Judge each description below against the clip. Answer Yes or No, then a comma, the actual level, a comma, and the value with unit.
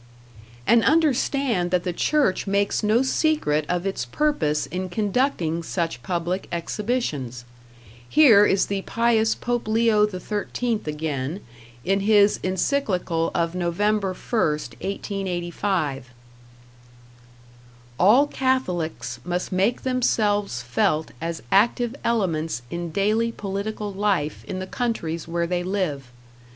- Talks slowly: Yes, slow, 115 wpm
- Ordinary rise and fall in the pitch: Yes, average, 4.9 semitones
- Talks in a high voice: Yes, high, 195 Hz